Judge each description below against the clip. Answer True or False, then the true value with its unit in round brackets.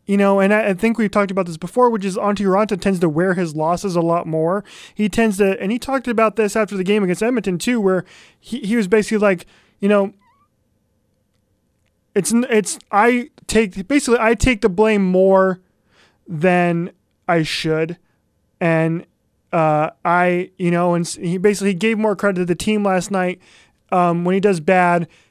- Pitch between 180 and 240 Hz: True (190 Hz)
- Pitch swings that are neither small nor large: True (3.5 semitones)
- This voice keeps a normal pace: True (185 wpm)